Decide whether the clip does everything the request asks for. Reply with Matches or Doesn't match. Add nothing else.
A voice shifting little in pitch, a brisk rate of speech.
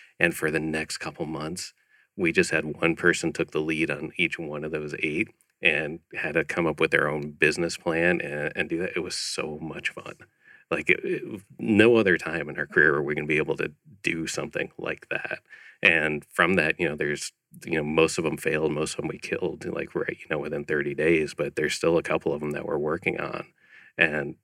Matches